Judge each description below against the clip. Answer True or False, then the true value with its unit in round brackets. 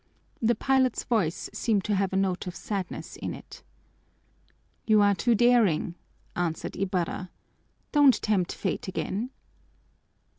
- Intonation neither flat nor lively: True (4.2 semitones)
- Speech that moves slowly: True (125 wpm)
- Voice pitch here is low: False (200 Hz)